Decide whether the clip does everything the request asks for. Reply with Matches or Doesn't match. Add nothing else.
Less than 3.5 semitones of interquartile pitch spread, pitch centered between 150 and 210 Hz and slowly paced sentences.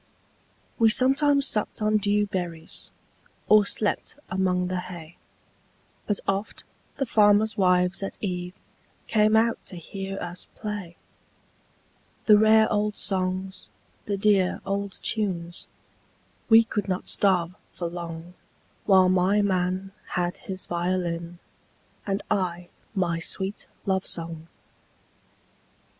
Matches